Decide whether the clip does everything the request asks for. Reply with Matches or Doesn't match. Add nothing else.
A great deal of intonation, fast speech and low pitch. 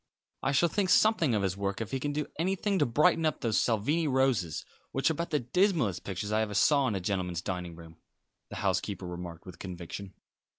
Matches